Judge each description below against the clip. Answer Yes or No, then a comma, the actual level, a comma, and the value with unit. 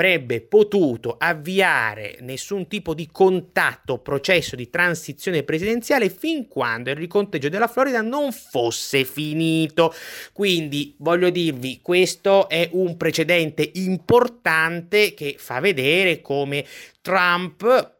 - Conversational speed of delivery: No, slow, 110 wpm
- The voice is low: No, medium, 170 Hz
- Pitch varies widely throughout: No, average, 4.8 semitones